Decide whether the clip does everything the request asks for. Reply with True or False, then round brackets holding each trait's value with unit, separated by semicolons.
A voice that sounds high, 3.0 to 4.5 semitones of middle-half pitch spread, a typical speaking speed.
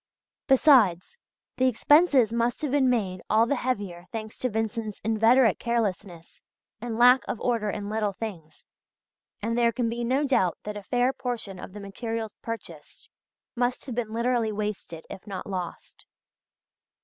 True (225 Hz; 3.3 semitones; 155 wpm)